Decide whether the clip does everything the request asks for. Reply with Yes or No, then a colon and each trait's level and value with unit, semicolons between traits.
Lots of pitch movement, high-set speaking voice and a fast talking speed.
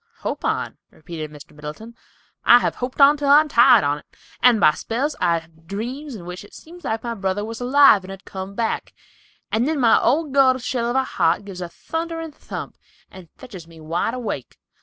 Yes: wide, 7.0 semitones; high, 225 Hz; fast, 210 wpm